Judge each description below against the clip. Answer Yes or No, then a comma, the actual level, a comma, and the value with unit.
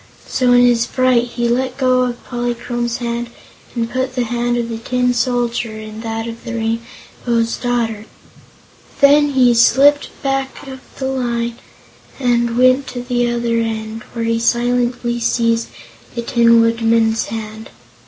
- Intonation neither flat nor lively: No, narrow, 1.3 semitones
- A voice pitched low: No, high, 240 Hz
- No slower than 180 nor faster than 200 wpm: No, average, 150 wpm